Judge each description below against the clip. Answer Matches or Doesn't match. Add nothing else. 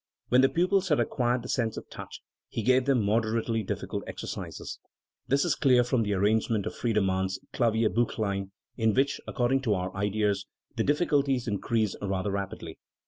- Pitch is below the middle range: Matches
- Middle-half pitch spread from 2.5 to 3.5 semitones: Doesn't match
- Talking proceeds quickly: Doesn't match